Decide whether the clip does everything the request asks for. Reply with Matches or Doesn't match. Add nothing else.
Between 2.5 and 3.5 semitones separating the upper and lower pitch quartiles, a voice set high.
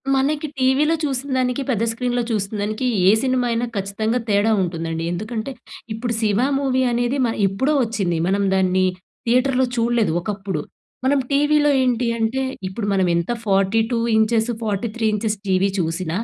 Doesn't match